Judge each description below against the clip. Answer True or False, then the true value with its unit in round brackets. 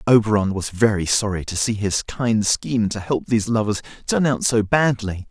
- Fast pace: False (190 wpm)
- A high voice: False (110 Hz)